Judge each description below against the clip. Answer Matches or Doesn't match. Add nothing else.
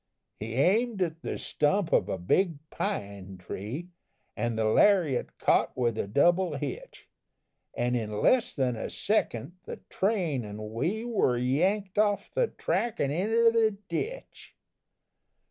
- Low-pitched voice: Doesn't match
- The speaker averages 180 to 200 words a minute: Doesn't match